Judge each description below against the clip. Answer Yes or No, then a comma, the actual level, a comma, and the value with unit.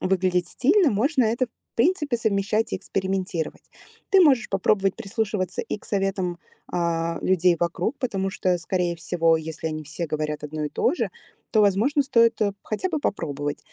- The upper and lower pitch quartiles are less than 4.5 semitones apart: No, average, 5.1 semitones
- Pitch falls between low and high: No, high, 195 Hz